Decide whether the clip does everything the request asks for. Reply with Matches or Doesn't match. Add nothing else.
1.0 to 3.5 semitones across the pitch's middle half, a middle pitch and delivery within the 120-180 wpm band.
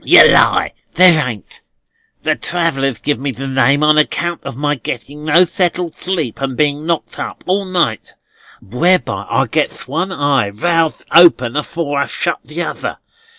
Doesn't match